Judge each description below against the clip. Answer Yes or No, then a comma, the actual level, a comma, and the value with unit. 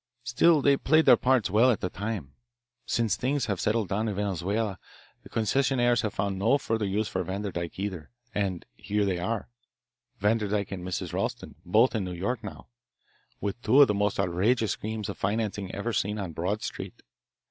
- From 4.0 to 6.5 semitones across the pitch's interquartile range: No, average, 3.1 semitones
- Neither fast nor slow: Yes, average, 180 wpm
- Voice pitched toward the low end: Yes, low, 105 Hz